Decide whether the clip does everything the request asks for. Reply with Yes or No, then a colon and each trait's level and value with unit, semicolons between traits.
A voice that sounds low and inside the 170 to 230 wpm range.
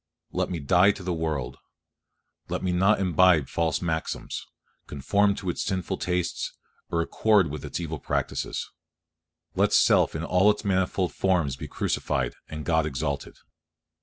No: very low, 85 Hz; average, 155 wpm